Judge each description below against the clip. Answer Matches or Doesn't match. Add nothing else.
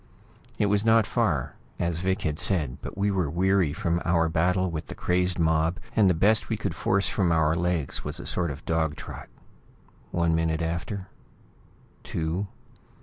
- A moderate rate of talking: Matches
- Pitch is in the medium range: Doesn't match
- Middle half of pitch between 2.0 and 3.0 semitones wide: Matches